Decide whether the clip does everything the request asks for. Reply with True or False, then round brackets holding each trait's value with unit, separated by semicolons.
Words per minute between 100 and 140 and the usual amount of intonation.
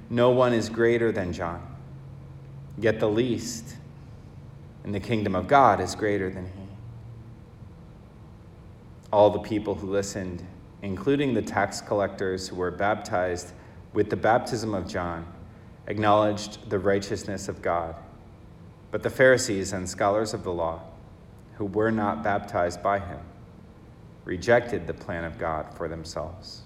True (135 wpm; 3.6 semitones)